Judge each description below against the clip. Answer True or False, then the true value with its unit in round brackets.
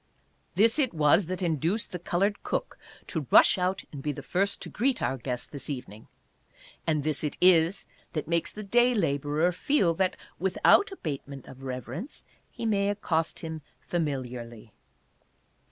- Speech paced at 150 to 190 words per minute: True (155 wpm)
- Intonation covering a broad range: True (5.7 semitones)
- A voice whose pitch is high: False (165 Hz)